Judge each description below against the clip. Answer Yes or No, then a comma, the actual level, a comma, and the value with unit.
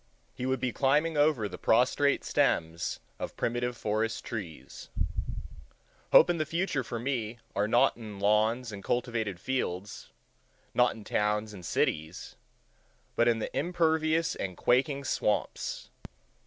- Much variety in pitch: No, average, 4.5 semitones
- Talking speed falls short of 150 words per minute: Yes, slow, 135 wpm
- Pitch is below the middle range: Yes, low, 120 Hz